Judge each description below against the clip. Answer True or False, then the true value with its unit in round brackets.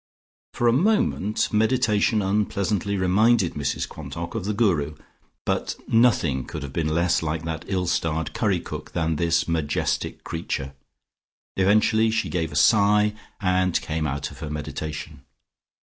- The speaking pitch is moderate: False (90 Hz)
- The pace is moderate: True (150 wpm)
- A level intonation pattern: False (5.1 semitones)